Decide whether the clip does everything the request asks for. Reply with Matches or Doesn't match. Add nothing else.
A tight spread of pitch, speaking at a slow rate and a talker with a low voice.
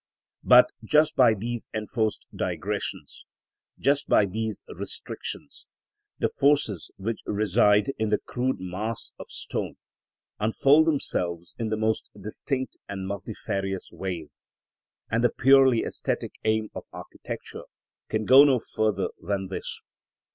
Doesn't match